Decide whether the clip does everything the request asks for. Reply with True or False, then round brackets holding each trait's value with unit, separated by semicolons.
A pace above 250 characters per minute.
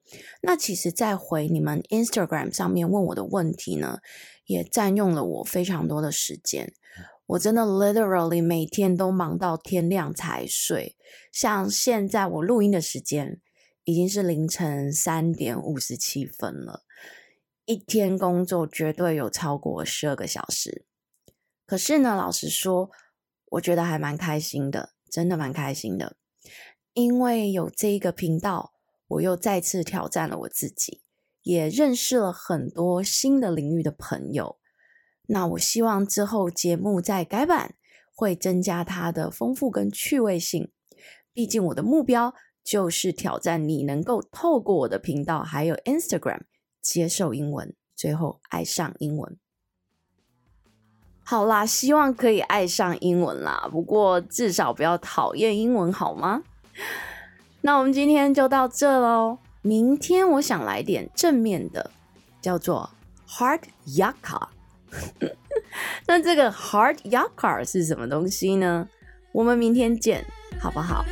False (240 characters per minute)